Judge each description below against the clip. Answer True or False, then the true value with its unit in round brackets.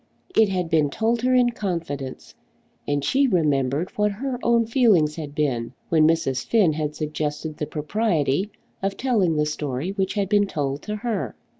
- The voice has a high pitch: False (165 Hz)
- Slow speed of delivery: False (170 wpm)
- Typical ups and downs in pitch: False (6.1 semitones)